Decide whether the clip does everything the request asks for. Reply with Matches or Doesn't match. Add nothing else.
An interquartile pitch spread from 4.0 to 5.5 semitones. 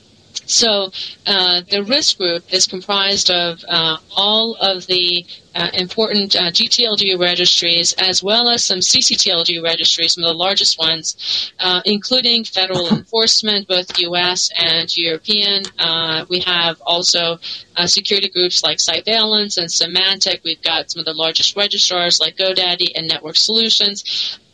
Doesn't match